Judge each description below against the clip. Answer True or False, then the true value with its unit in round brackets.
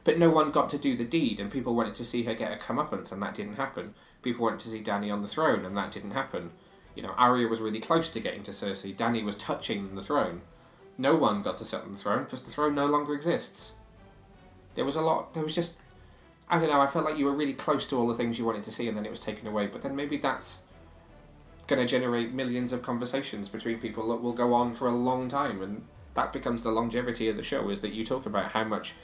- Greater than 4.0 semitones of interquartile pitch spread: True (4.4 semitones)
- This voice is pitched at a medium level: False (120 Hz)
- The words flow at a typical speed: False (265 wpm)